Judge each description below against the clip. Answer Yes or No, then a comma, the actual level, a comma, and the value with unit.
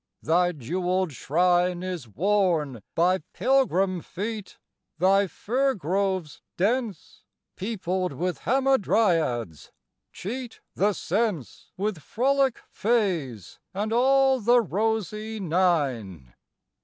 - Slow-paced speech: Yes, slow, 90 wpm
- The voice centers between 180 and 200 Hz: Yes, high, 190 Hz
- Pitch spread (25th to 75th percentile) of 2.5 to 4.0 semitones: No, average, 4.8 semitones